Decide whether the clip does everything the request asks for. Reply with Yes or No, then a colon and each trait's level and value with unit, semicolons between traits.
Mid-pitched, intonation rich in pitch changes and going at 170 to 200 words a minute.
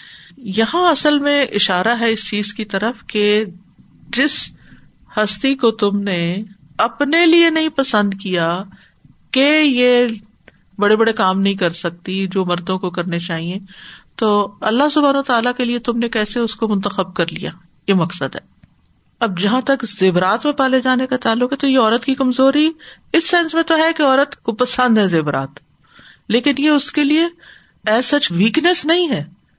No: high, 225 Hz; wide, 6.0 semitones; average, 175 wpm